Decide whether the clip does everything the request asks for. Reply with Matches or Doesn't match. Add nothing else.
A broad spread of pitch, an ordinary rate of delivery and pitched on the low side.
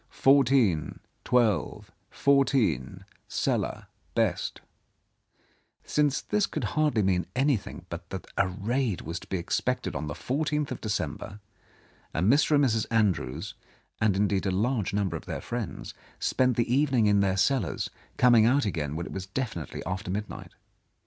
Matches